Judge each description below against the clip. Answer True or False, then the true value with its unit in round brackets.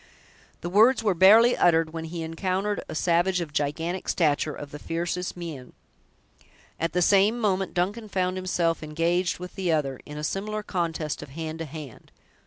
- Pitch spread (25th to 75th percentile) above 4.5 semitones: False (3.0 semitones)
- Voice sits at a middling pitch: True (170 Hz)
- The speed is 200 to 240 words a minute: False (175 wpm)